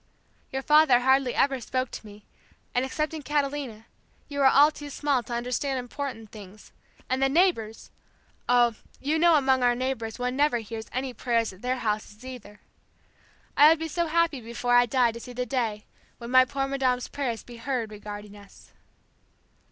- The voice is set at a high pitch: Yes, very high, 250 Hz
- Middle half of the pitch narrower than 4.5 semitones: Yes, average, 3.2 semitones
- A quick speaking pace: No, average, 175 wpm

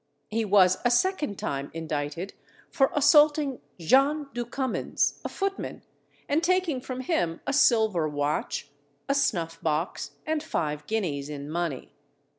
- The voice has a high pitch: Yes, high, 220 Hz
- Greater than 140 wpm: No, slow, 135 wpm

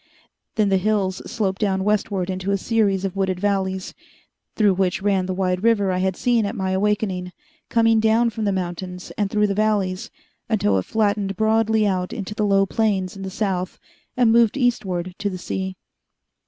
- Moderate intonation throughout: No, narrow, 2.3 semitones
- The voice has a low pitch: No, high, 195 Hz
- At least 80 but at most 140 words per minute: No, average, 185 wpm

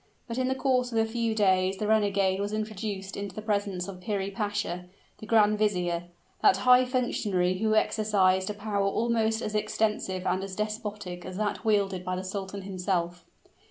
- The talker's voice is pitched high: Yes, high, 205 Hz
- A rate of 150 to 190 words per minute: Yes, average, 180 wpm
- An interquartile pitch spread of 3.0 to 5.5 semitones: No, narrow, 2.5 semitones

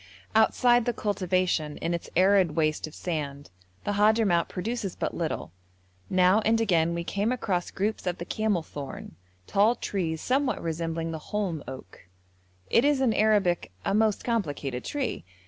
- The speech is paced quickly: No, average, 150 wpm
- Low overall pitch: No, medium, 185 Hz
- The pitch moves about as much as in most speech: Yes, average, 5.0 semitones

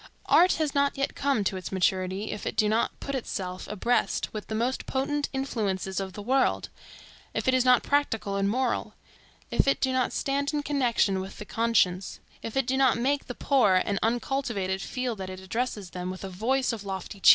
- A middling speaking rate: No, fast, 210 wpm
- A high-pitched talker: Yes, high, 230 Hz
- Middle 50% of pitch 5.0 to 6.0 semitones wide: Yes, wide, 5.6 semitones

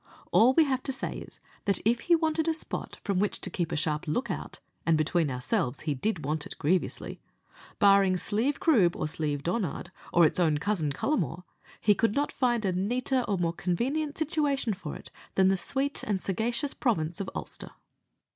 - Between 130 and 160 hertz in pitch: No, high, 195 Hz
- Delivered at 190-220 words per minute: Yes, average, 195 wpm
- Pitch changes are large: Yes, wide, 7.3 semitones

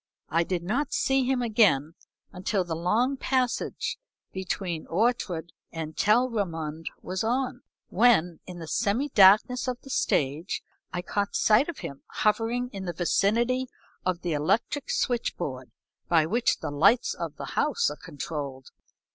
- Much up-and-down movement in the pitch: Yes, wide, 6.7 semitones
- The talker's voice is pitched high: Yes, high, 195 Hz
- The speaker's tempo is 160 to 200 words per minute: No, average, 145 wpm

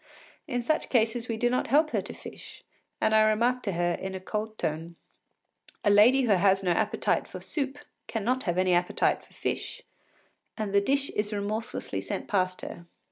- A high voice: Yes, high, 215 Hz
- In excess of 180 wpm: Yes, average, 190 wpm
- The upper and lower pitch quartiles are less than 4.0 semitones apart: No, average, 4.3 semitones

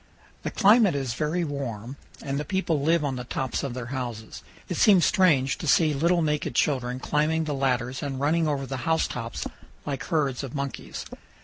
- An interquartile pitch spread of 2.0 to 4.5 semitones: Yes, average, 3.7 semitones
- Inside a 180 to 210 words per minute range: Yes, average, 190 wpm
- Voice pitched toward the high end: No, medium, 140 Hz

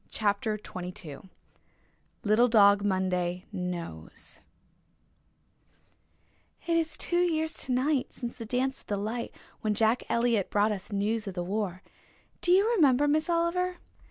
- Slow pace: Yes, slow, 130 wpm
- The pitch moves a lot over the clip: Yes, wide, 6.6 semitones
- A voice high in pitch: Yes, high, 220 Hz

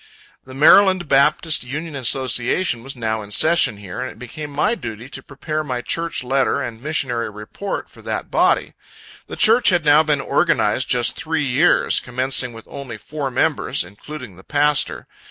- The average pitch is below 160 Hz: Yes, low, 135 Hz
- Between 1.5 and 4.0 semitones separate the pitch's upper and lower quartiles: No, average, 4.4 semitones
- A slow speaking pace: No, average, 170 wpm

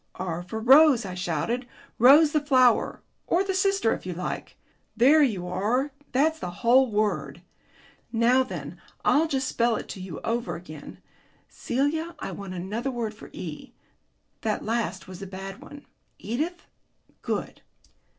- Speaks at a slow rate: No, average, 150 wpm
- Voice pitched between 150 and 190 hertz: No, high, 235 Hz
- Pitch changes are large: Yes, wide, 6.6 semitones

